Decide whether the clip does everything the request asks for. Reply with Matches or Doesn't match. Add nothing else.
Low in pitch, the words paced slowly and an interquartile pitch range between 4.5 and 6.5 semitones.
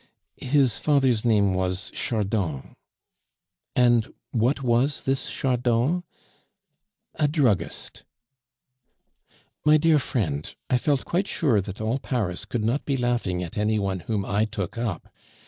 Matches